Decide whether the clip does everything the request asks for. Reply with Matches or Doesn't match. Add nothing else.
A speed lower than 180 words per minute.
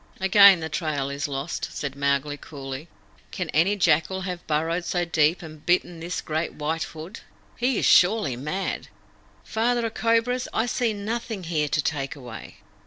Matches